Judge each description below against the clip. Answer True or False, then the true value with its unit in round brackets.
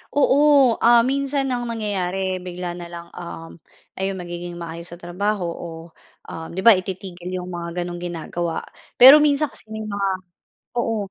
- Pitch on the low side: False (185 Hz)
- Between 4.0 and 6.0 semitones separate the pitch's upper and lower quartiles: True (5.0 semitones)